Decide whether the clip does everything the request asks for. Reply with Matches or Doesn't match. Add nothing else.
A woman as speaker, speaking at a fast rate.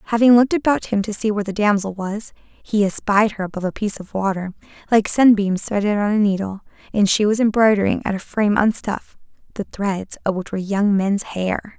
Matches